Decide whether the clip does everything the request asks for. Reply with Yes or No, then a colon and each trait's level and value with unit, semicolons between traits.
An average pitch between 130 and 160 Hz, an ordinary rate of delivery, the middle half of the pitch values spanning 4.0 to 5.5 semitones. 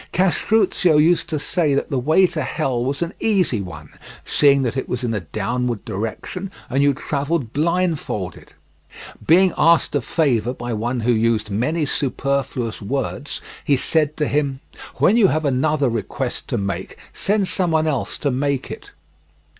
Yes: medium, 140 Hz; average, 160 wpm; average, 4.9 semitones